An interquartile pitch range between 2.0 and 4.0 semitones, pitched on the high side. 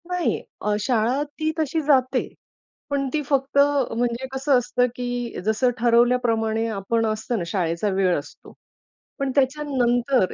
Yes: average, 3.7 semitones; high, 245 Hz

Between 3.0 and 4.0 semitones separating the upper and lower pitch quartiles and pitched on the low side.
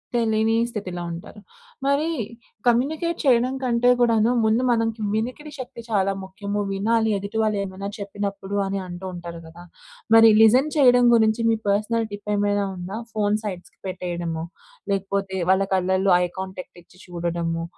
No: average, 3.4 semitones; high, 205 Hz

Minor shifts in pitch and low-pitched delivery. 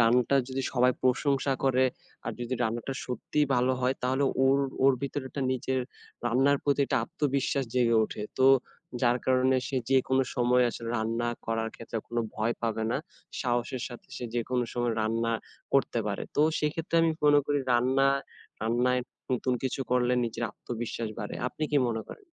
Yes: narrow, 2.3 semitones; low, 125 Hz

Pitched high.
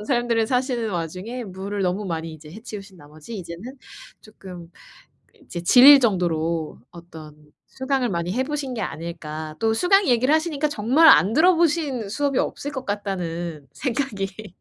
Yes: high, 210 Hz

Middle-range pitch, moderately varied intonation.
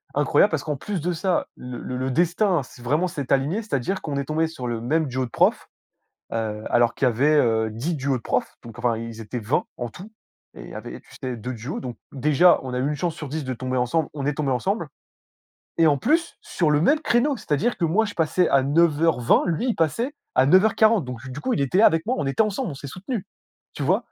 No: medium, 145 Hz; wide, 5.9 semitones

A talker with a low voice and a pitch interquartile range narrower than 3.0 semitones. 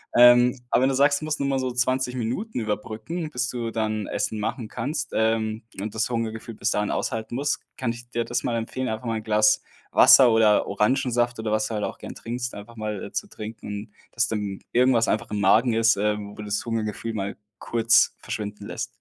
Yes: low, 115 Hz; narrow, 2.4 semitones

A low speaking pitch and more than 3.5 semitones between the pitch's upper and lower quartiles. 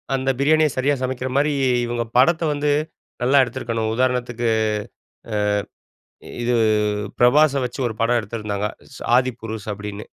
No: low, 125 Hz; average, 2.8 semitones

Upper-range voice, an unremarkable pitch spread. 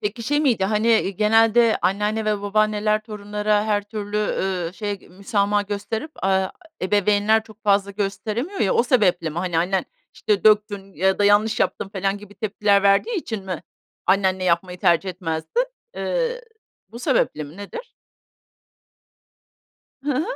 No: high, 205 Hz; narrow, 2.1 semitones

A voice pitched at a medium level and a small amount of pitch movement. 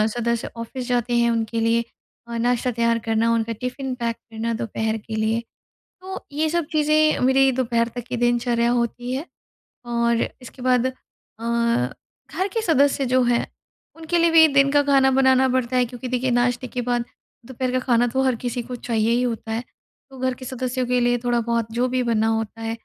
No: high, 245 Hz; narrow, 2.0 semitones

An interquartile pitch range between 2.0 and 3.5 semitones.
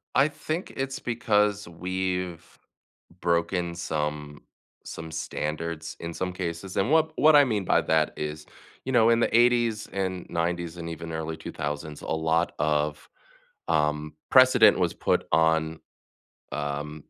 No: average, 4.7 semitones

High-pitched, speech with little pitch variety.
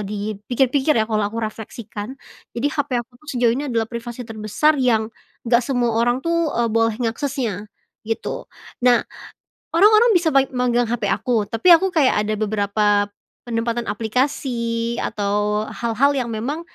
No: high, 235 Hz; average, 3.5 semitones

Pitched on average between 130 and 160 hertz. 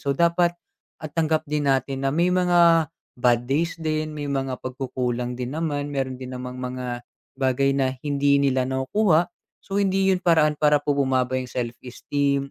Yes: medium, 140 Hz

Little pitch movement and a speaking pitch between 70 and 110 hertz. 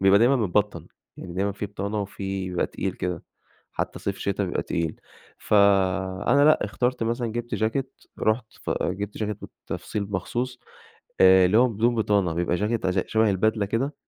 No: average, 3.2 semitones; low, 100 Hz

